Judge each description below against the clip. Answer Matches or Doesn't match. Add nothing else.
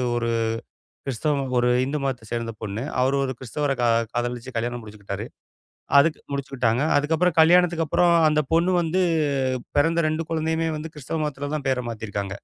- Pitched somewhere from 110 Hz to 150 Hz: Matches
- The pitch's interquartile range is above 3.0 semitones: Matches